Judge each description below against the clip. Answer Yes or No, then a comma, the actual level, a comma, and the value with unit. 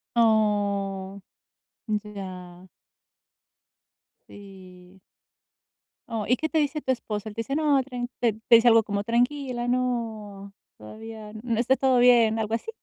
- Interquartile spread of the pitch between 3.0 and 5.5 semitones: Yes, average, 3.4 semitones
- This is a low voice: No, high, 220 Hz